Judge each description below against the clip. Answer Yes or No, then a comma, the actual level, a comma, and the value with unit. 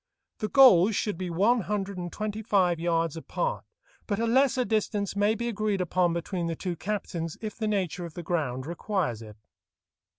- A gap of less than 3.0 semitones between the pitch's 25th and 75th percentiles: No, average, 4.0 semitones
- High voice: Yes, high, 195 Hz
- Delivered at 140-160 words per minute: No, average, 185 wpm